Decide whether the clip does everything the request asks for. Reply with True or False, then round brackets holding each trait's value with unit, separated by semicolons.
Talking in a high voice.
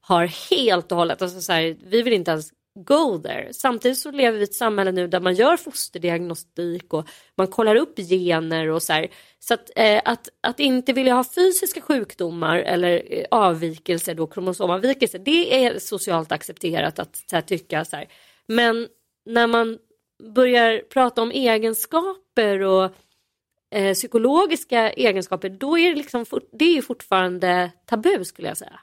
True (220 Hz)